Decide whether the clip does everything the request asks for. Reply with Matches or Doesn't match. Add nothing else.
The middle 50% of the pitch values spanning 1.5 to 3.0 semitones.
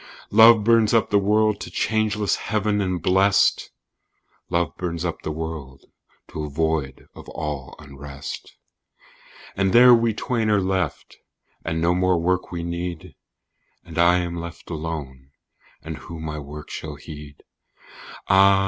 Doesn't match